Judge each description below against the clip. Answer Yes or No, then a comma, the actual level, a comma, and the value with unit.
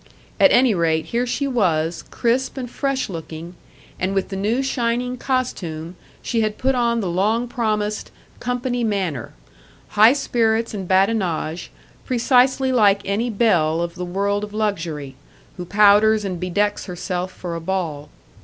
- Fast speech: No, average, 150 wpm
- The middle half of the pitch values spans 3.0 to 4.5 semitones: No, average, 5.1 semitones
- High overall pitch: Yes, high, 205 Hz